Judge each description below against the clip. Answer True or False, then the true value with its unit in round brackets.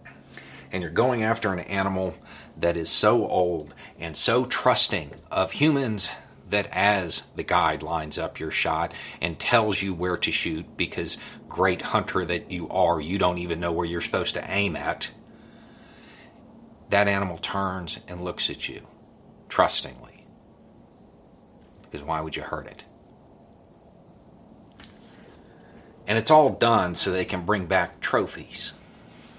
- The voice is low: True (95 Hz)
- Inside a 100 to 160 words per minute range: True (140 wpm)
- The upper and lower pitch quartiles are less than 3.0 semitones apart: False (3.5 semitones)